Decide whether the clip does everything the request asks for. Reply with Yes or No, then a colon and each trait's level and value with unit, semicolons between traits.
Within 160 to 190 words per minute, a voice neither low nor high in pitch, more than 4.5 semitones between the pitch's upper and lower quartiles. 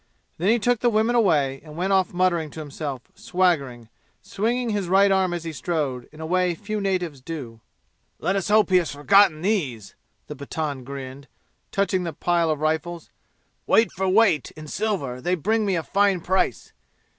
Yes: average, 185 wpm; medium, 175 Hz; average, 4.9 semitones